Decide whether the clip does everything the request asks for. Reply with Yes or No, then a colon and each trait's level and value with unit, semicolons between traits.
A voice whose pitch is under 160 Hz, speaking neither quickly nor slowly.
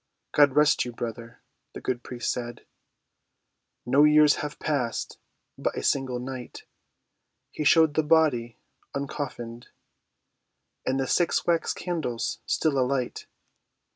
No: low, 135 Hz; slow, 115 wpm